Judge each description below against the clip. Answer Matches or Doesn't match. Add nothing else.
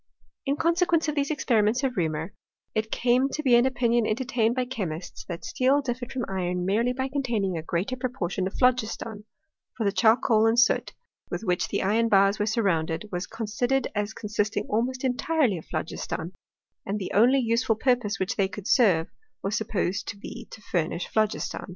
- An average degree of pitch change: Matches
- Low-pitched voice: Doesn't match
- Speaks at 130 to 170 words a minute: Doesn't match